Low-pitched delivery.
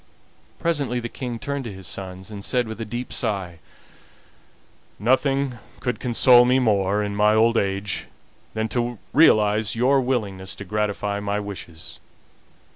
Yes: low, 110 Hz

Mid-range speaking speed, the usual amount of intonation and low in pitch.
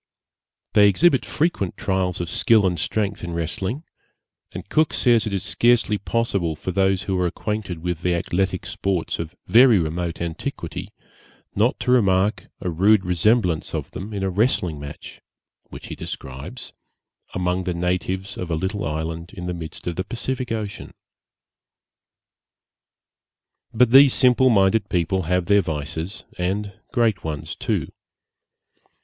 Yes: average, 145 wpm; average, 3.8 semitones; very low, 95 Hz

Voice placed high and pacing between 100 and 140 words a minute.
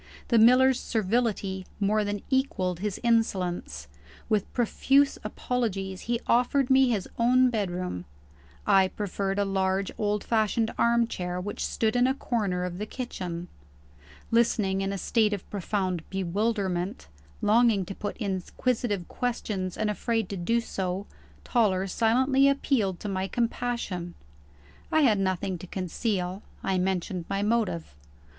Yes: high, 205 Hz; slow, 135 wpm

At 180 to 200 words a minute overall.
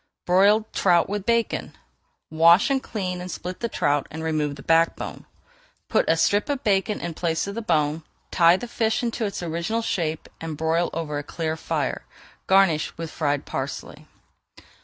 No: average, 170 wpm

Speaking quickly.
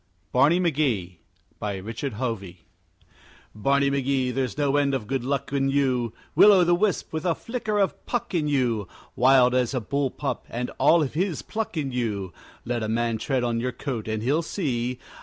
No: average, 190 wpm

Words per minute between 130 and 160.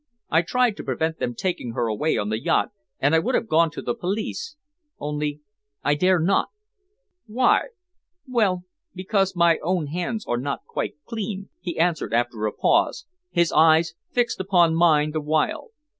No: average, 170 wpm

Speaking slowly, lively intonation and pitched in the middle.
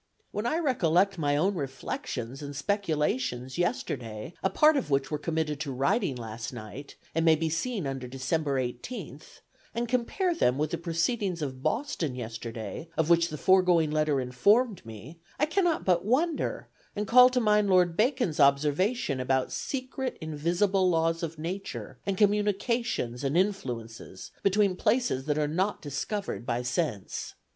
No: average, 155 wpm; wide, 7.2 semitones; medium, 165 Hz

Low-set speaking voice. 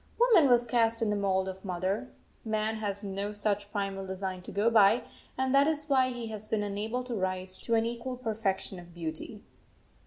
No: high, 210 Hz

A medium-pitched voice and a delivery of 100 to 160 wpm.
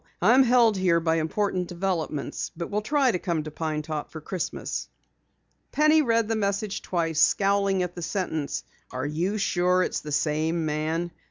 No: medium, 180 Hz; average, 180 wpm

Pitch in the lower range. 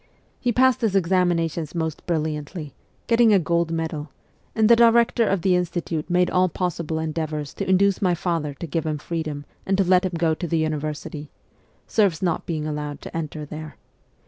No: medium, 170 Hz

